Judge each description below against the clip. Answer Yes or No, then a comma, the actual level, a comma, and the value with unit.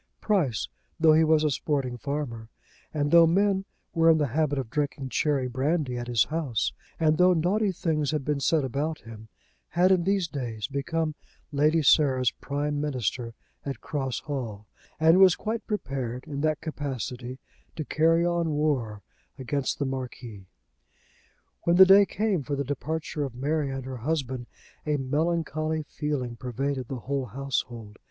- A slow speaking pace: No, average, 160 wpm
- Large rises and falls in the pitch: No, average, 3.8 semitones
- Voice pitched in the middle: Yes, medium, 145 Hz